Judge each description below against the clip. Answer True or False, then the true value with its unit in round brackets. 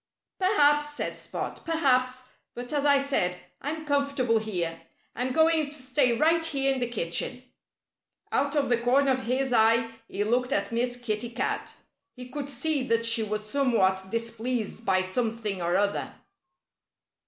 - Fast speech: False (155 wpm)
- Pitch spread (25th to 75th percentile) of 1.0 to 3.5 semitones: False (3.9 semitones)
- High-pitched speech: True (250 Hz)